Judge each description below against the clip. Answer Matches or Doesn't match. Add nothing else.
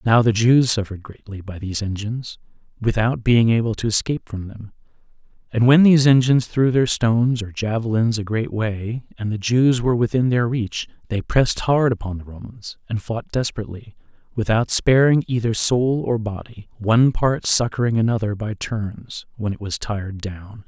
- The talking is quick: Doesn't match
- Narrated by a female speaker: Doesn't match